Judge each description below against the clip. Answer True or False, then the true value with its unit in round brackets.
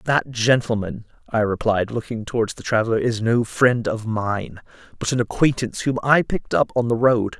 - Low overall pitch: True (115 Hz)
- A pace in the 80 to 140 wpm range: False (185 wpm)